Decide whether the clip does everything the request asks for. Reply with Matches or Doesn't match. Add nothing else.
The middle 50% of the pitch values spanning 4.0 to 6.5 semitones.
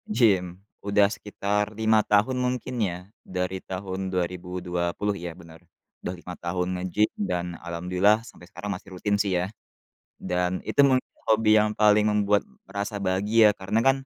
Doesn't match